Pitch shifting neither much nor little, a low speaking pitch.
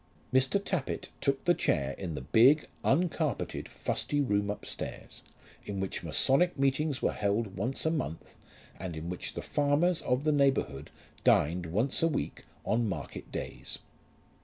No: wide, 7.5 semitones; low, 125 Hz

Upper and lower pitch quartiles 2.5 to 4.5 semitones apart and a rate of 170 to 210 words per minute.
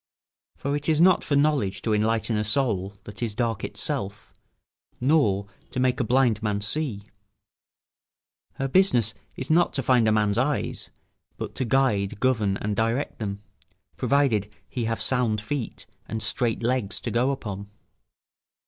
No: average, 4.2 semitones; average, 155 wpm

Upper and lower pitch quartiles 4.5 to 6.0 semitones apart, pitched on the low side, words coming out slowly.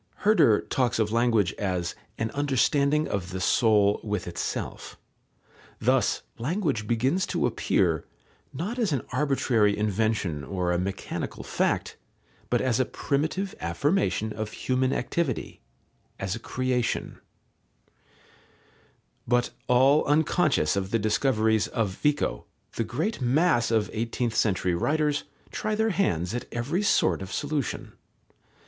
Yes: wide, 5.6 semitones; low, 120 Hz; slow, 125 wpm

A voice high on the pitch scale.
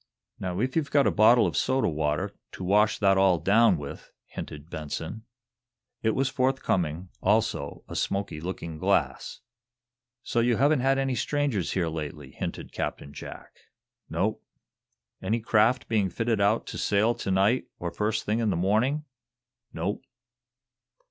No: low, 105 Hz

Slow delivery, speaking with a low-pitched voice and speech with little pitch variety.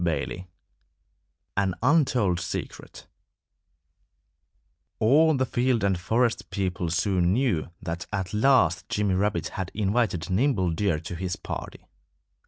No: slow, 115 wpm; low, 100 Hz; average, 5.1 semitones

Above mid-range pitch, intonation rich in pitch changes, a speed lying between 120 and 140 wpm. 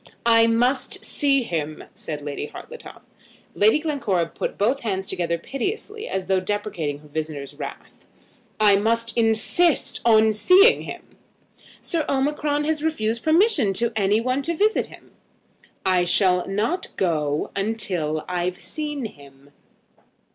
Yes: high, 220 Hz; wide, 7.9 semitones; slow, 135 wpm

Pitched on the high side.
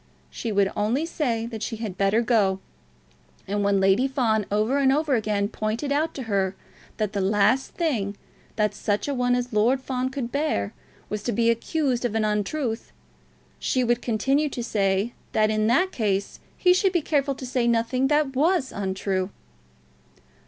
Yes: high, 230 Hz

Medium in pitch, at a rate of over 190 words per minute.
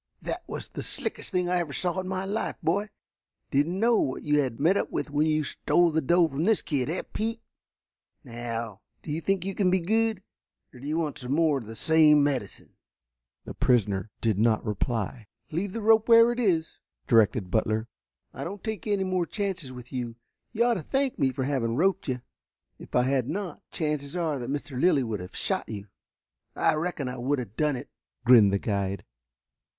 Yes: medium, 150 Hz; fast, 205 wpm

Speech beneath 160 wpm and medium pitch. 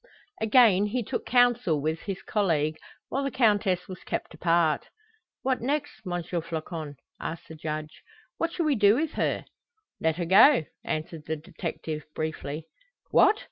Yes: average, 150 wpm; medium, 180 Hz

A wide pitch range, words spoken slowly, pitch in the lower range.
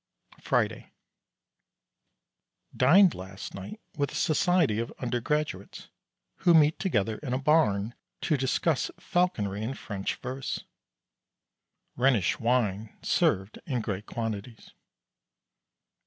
Yes: wide, 6.4 semitones; slow, 100 wpm; low, 125 Hz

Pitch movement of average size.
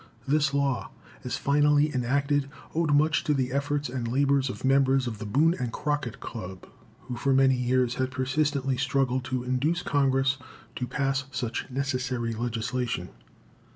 No: narrow, 2.2 semitones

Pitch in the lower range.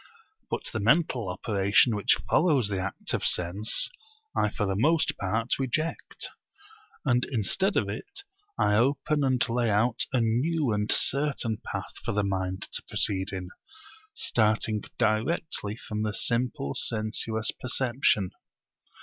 Yes: low, 110 Hz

